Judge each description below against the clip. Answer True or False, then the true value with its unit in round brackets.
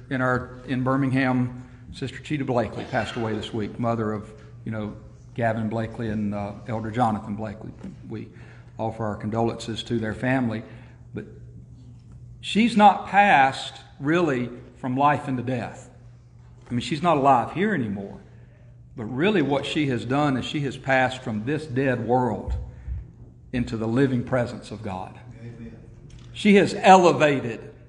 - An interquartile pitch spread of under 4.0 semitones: True (2.8 semitones)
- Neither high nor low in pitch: False (120 Hz)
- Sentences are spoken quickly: False (145 wpm)